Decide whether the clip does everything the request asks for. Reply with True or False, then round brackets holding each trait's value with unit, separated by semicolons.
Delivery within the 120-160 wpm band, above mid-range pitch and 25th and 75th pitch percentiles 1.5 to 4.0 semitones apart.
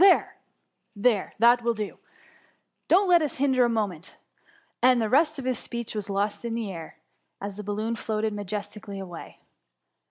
False (170 wpm; 220 Hz; 3.5 semitones)